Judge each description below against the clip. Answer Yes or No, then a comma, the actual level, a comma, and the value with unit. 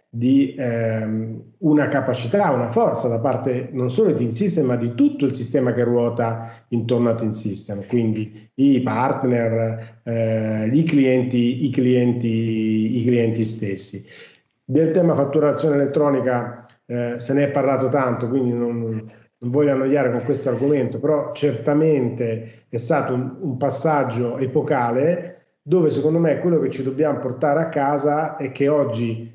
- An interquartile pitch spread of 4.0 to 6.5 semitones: No, average, 3.6 semitones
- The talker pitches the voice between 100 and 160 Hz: Yes, low, 125 Hz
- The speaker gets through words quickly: No, average, 145 wpm